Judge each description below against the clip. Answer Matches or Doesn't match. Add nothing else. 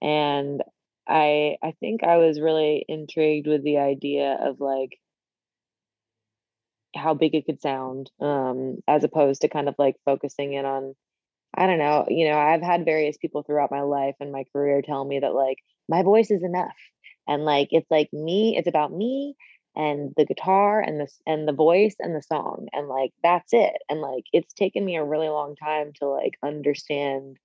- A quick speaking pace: Doesn't match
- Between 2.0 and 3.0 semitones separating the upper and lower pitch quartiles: Matches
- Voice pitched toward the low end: Doesn't match